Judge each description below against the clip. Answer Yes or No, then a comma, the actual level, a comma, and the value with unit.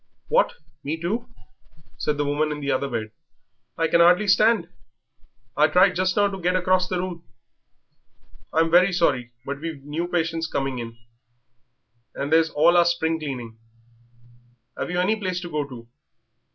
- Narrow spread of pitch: No, average, 3.8 semitones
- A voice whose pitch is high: No, medium, 165 Hz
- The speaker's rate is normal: Yes, average, 160 wpm